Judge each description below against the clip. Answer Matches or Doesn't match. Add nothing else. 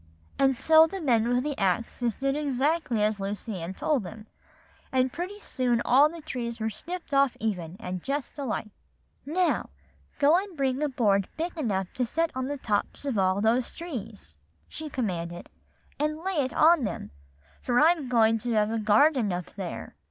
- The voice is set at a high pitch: Matches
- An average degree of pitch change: Doesn't match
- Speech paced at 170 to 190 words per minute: Matches